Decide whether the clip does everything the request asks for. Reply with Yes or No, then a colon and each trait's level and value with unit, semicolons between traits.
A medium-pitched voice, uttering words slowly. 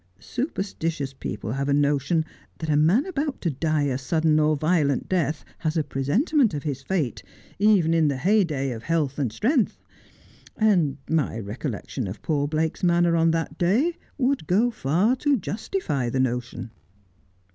No: medium, 155 Hz; average, 165 wpm